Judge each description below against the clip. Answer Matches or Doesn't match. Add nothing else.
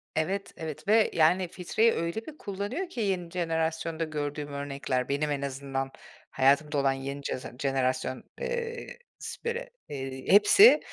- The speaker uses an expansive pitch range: Matches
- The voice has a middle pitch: Matches